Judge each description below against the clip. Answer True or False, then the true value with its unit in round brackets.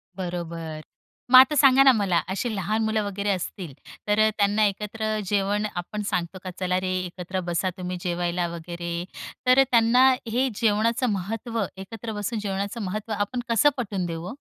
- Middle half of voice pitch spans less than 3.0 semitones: False (3.7 semitones)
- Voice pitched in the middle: False (205 Hz)